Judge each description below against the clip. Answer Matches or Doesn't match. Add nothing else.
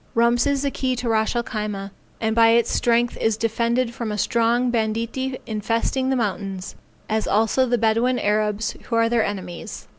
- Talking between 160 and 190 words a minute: Matches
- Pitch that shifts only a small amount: Matches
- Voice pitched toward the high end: Matches